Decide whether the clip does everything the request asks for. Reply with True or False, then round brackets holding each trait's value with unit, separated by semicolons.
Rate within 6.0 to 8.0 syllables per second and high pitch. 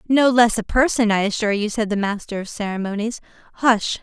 True (6.2 syllables/s; 220 Hz)